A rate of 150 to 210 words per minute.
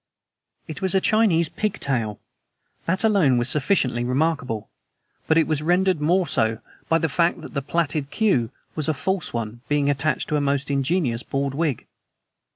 Yes: average, 165 wpm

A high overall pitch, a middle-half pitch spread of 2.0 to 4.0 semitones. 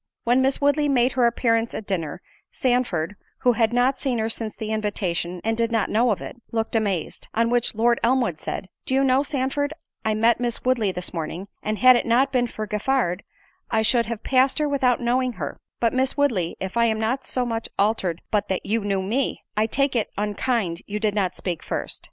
Yes: high, 230 Hz; average, 3.5 semitones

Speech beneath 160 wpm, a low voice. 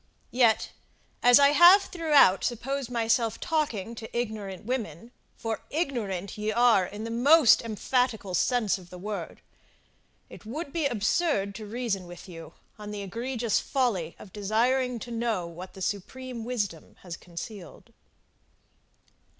No: average, 140 wpm; high, 225 Hz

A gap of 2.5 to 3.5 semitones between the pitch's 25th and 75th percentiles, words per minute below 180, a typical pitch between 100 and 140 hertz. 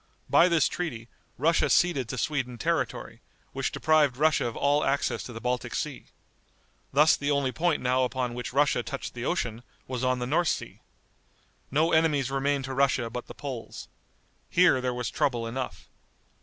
Yes: average, 3.2 semitones; average, 170 wpm; low, 135 Hz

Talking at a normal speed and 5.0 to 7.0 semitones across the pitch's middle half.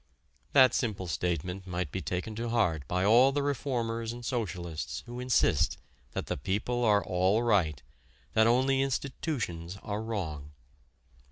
Yes: average, 145 wpm; average, 5.3 semitones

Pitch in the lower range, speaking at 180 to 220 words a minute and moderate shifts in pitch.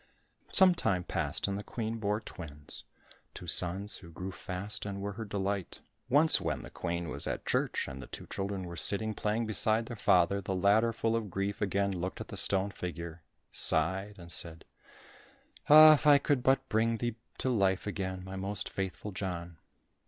Yes: low, 100 Hz; average, 185 wpm; average, 3.2 semitones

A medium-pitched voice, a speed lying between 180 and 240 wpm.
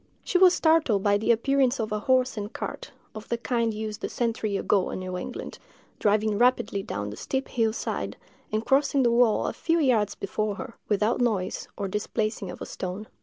No: high, 220 Hz; average, 200 wpm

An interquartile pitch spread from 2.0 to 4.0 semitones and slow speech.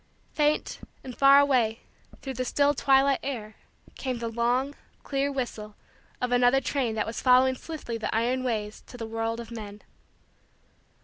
No: average, 3.1 semitones; average, 160 wpm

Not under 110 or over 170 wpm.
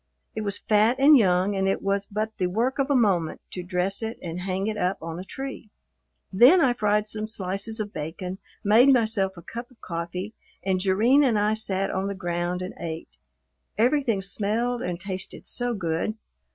No: average, 190 wpm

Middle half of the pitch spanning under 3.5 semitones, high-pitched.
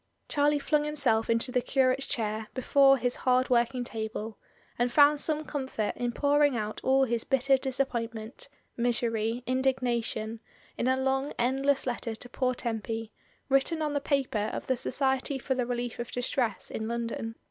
Yes: average, 2.8 semitones; very high, 250 Hz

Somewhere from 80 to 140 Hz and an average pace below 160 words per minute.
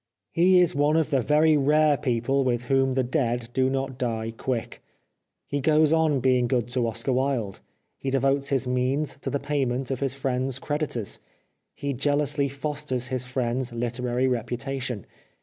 No: low, 135 Hz; average, 165 wpm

